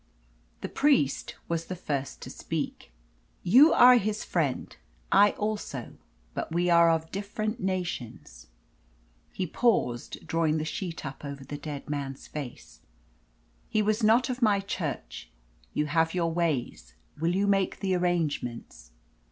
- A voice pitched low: No, medium, 170 Hz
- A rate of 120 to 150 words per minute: Yes, average, 140 wpm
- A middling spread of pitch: No, wide, 5.8 semitones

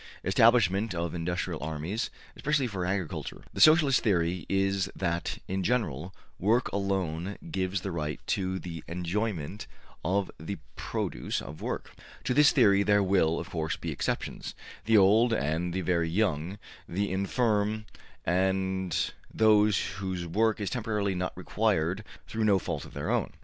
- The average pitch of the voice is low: Yes, very low, 95 Hz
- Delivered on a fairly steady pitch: No, average, 3.5 semitones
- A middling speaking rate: Yes, average, 150 wpm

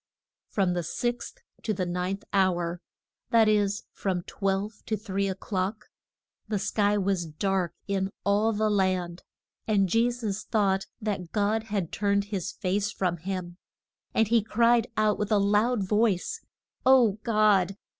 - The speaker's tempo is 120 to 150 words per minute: Yes, average, 145 wpm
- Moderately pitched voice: No, high, 200 Hz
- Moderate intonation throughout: No, narrow, 2.3 semitones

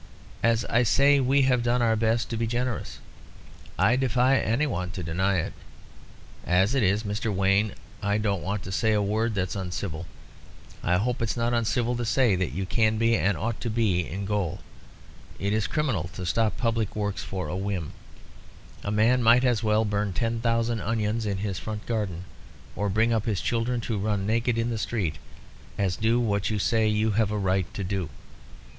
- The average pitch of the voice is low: Yes, low, 110 Hz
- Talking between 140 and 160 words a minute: No, average, 195 wpm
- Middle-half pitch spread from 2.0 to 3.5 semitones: Yes, average, 3.0 semitones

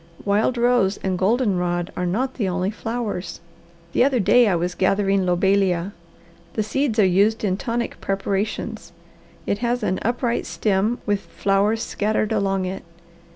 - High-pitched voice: Yes, high, 200 Hz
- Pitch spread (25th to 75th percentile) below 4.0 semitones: Yes, average, 3.3 semitones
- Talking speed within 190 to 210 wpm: No, average, 155 wpm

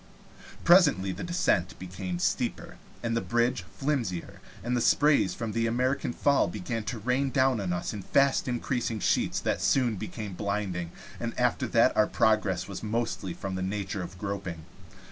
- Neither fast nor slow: Yes, average, 165 wpm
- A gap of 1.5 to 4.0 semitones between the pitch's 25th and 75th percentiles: No, average, 4.9 semitones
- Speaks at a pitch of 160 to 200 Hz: No, low, 110 Hz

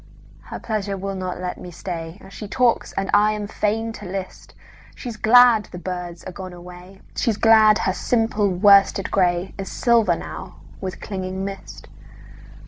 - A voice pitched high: Yes, high, 195 Hz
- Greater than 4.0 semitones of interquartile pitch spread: No, average, 2.8 semitones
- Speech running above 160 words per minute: No, average, 140 wpm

